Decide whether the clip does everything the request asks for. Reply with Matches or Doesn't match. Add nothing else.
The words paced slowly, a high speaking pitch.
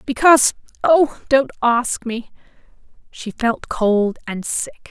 Matches